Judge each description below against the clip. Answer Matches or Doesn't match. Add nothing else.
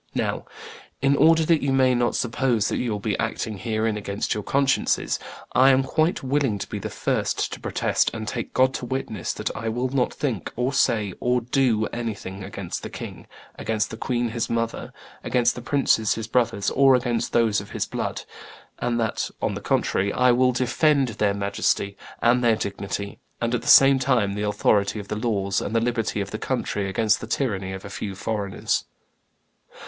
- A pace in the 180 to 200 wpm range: Matches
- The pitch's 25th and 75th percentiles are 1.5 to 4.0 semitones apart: Matches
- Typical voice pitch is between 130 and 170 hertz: Doesn't match